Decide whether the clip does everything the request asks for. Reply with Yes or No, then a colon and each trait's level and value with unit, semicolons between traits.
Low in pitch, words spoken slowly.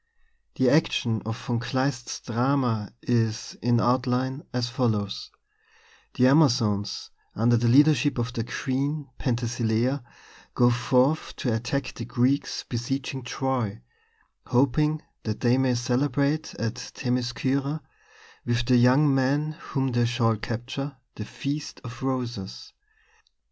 Yes: low, 125 Hz; slow, 120 wpm